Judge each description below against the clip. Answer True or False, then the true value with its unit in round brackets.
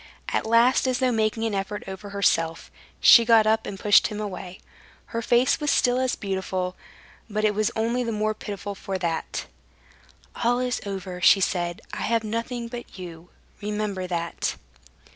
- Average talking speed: True (170 wpm)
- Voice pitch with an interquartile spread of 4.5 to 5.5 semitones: False (3.5 semitones)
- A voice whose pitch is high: True (210 Hz)